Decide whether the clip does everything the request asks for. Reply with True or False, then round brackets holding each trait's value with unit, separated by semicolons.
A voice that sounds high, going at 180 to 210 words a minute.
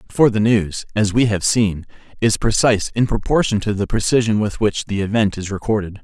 False (105 Hz; 200 wpm)